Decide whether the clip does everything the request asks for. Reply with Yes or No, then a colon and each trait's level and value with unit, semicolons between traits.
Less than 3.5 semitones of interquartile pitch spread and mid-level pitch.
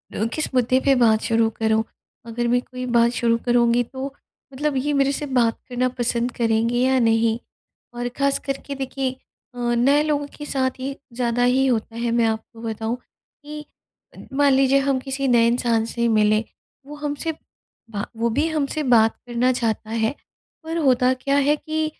No: average, 2.9 semitones; very high, 250 Hz